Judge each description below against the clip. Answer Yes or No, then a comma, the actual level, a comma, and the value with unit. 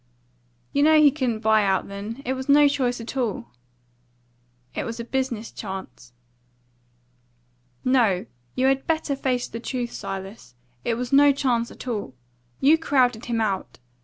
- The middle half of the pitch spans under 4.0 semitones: Yes, average, 3.6 semitones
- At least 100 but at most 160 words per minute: Yes, average, 155 wpm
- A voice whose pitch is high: Yes, high, 245 Hz